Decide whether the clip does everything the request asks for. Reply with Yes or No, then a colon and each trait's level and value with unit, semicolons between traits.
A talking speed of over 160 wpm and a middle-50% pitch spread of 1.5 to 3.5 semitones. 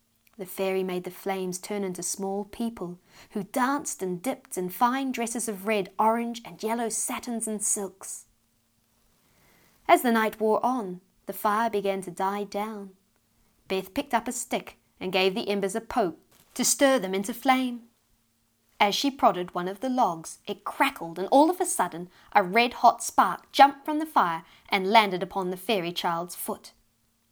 No: average, 175 wpm; average, 4.4 semitones